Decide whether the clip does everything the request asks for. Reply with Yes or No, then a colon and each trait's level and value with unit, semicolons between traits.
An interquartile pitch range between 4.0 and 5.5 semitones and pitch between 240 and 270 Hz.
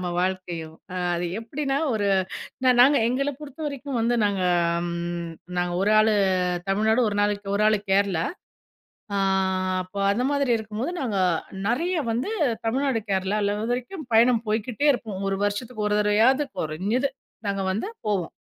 No: average, 4.5 semitones; high, 215 Hz